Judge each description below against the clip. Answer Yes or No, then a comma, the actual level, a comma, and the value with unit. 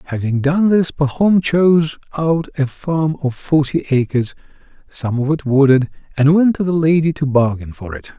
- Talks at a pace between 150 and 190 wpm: Yes, average, 175 wpm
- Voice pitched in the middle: Yes, medium, 145 Hz